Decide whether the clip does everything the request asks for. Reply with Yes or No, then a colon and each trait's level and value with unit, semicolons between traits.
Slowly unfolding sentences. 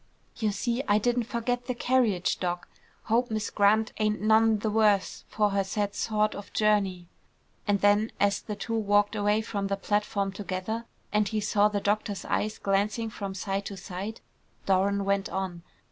No: average, 175 wpm